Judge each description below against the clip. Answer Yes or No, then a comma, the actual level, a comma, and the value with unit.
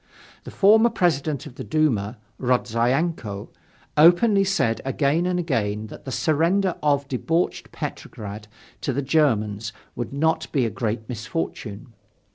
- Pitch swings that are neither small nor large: No, wide, 6.3 semitones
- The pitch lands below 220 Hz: Yes, medium, 140 Hz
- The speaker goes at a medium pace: No, slow, 130 wpm